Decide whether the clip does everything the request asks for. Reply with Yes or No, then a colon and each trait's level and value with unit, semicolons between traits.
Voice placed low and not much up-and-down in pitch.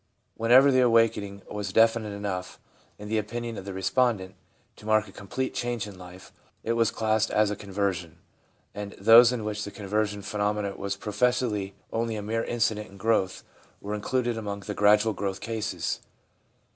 Yes: low, 105 Hz; narrow, 2.2 semitones